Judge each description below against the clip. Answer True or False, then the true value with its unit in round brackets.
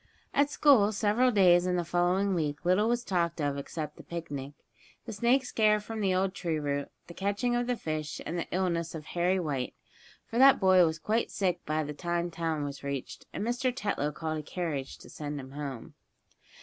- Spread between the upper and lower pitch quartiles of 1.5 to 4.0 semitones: False (5.4 semitones)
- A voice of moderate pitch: True (175 Hz)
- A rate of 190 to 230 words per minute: True (200 wpm)